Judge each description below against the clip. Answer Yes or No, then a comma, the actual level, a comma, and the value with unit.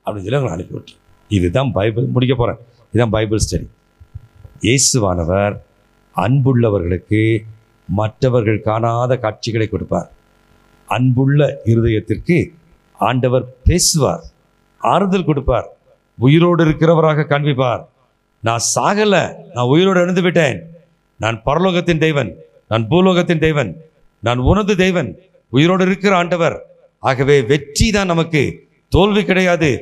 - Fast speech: No, average, 100 wpm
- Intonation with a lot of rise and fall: Yes, wide, 7.4 semitones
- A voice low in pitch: Yes, low, 130 Hz